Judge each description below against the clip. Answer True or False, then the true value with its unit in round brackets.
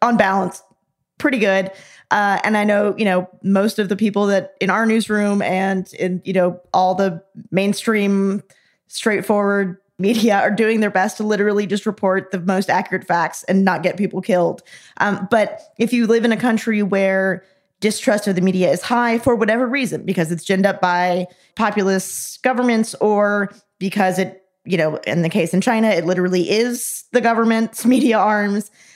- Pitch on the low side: False (200 Hz)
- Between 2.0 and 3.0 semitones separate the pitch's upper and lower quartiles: True (2.7 semitones)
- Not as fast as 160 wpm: False (180 wpm)